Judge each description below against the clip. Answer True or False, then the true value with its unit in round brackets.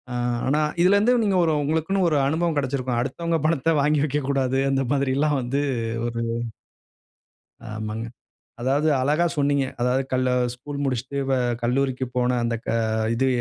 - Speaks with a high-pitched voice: False (140 Hz)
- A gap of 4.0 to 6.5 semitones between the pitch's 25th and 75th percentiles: False (3.0 semitones)